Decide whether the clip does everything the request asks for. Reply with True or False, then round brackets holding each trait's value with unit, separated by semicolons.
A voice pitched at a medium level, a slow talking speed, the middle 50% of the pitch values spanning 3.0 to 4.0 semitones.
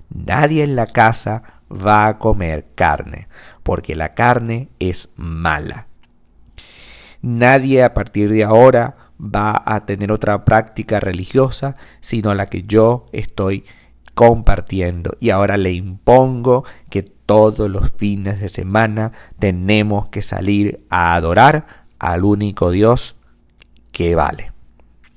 False (105 Hz; 120 wpm; 3.7 semitones)